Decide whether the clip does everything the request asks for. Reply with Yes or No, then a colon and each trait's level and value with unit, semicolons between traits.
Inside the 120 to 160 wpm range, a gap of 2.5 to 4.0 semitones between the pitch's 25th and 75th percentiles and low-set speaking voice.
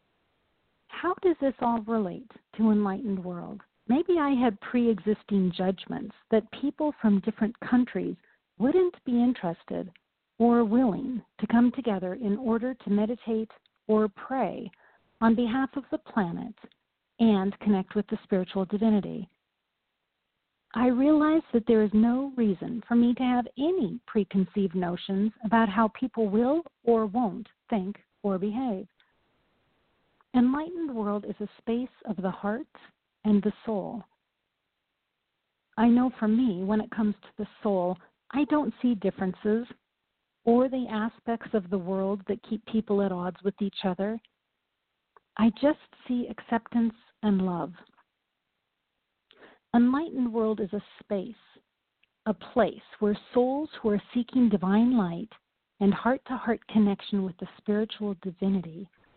No: slow, 135 wpm; average, 3.2 semitones; high, 225 Hz